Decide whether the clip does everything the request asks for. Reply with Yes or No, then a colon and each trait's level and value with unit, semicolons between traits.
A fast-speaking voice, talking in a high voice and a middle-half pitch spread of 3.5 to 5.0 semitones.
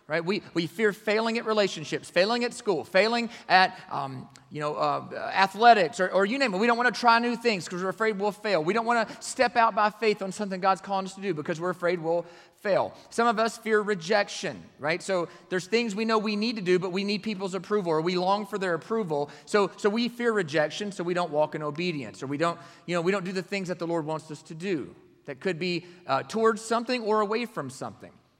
Yes: fast, 250 wpm; high, 195 Hz; average, 4.3 semitones